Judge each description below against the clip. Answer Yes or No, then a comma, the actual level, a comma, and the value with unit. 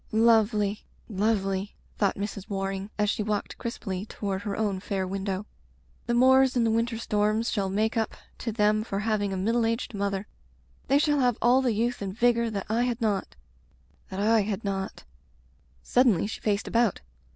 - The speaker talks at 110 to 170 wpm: No, average, 185 wpm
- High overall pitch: Yes, high, 210 Hz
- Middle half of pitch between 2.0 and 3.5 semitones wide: Yes, average, 2.7 semitones